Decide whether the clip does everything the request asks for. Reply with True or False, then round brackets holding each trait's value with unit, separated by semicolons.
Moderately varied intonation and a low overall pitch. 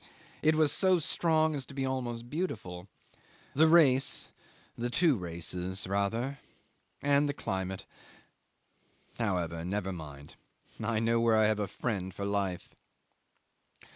False (7.0 semitones; 115 Hz)